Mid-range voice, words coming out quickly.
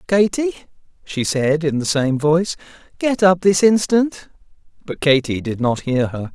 No: medium, 165 Hz; average, 160 wpm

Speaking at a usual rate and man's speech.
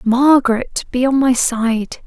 No: average, 145 wpm; female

